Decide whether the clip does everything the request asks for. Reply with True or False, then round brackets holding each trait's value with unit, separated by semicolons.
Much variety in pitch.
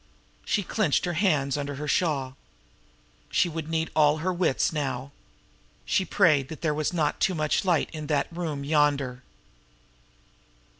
False (2.9 semitones)